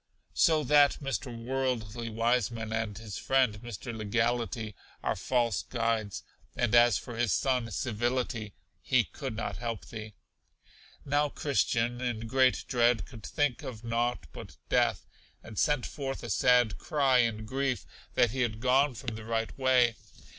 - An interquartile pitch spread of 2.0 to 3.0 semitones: Yes, narrow, 2.6 semitones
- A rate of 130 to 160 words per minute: Yes, average, 150 wpm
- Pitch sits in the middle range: No, low, 120 Hz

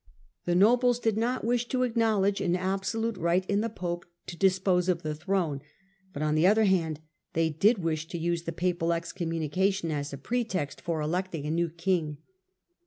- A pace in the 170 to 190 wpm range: Yes, average, 180 wpm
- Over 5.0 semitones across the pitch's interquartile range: No, average, 3.6 semitones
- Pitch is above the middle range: No, medium, 180 Hz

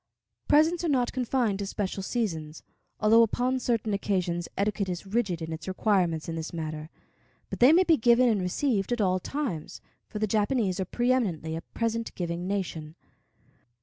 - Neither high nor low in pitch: No, high, 205 Hz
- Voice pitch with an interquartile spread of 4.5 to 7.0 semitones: Yes, wide, 5.6 semitones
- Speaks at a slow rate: No, average, 170 wpm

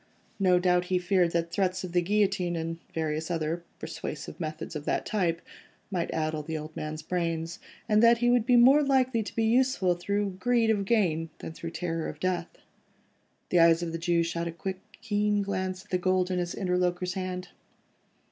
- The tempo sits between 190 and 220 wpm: Yes, average, 195 wpm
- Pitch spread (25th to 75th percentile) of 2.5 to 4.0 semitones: Yes, average, 3.3 semitones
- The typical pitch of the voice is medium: Yes, medium, 180 Hz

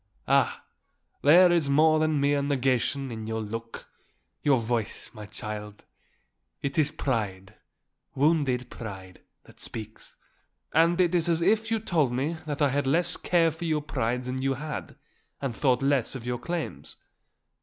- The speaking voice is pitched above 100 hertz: Yes, medium, 140 Hz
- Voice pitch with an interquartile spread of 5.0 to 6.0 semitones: Yes, average, 5.3 semitones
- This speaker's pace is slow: No, average, 155 wpm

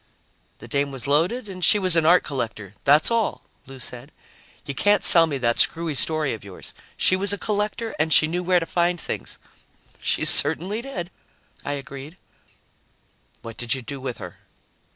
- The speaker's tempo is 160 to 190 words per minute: Yes, average, 180 wpm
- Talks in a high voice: No, medium, 160 Hz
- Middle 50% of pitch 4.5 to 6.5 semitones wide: Yes, average, 5.2 semitones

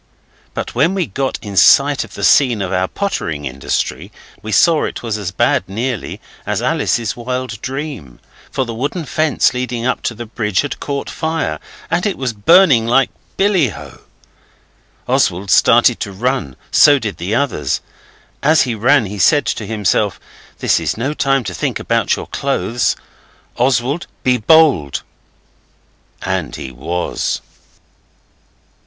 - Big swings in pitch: Yes, wide, 5.9 semitones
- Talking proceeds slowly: No, average, 150 wpm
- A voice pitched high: No, low, 120 Hz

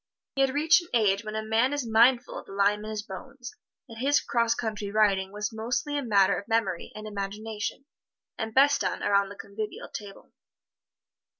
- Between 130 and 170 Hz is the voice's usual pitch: No, high, 220 Hz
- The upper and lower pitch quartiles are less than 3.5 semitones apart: Yes, average, 3.1 semitones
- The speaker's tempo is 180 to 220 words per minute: Yes, average, 190 wpm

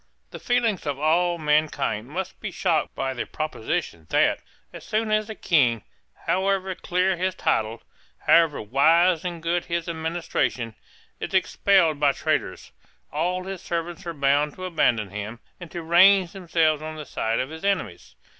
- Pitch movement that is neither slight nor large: Yes, average, 4.1 semitones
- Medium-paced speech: Yes, average, 160 wpm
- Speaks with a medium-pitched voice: Yes, medium, 165 Hz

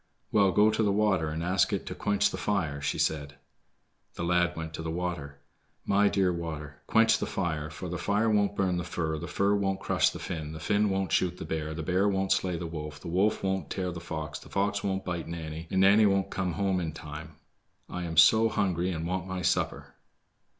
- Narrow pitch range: No, average, 3.4 semitones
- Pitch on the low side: Yes, very low, 90 Hz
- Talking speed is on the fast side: Yes, fast, 225 wpm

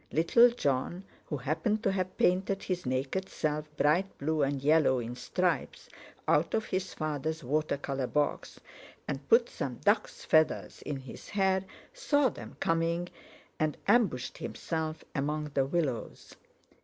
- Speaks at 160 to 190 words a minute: No, average, 140 wpm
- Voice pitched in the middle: Yes, medium, 155 Hz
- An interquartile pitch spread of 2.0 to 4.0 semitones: No, average, 5.1 semitones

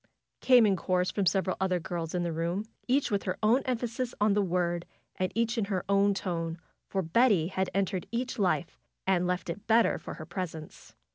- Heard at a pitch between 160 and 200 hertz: Yes, high, 190 Hz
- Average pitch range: Yes, average, 3.6 semitones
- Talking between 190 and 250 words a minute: Yes, average, 200 wpm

